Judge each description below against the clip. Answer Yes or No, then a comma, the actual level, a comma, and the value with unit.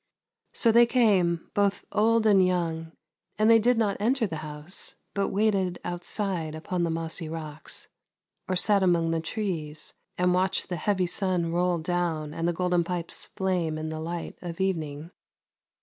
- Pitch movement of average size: Yes, average, 3.3 semitones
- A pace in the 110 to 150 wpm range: No, average, 165 wpm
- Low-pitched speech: No, medium, 175 Hz